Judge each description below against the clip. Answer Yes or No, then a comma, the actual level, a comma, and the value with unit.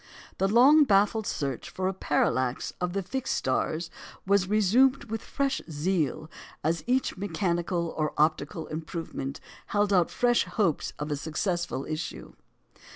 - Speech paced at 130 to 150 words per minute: Yes, average, 140 wpm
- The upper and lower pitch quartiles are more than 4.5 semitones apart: Yes, average, 5.0 semitones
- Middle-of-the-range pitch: Yes, medium, 180 Hz